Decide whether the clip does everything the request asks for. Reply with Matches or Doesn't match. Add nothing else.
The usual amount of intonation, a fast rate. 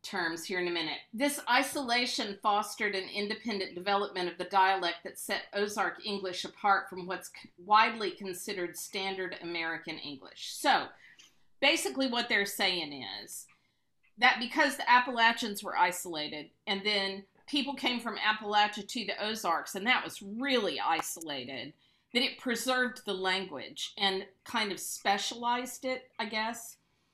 Doesn't match